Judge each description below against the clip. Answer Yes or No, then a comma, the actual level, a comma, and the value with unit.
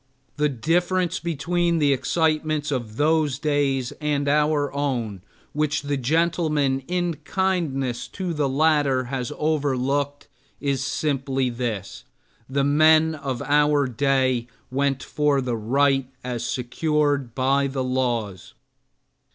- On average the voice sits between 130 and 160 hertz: Yes, medium, 140 Hz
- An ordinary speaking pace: No, slow, 120 wpm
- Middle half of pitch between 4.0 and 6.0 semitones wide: No, average, 2.8 semitones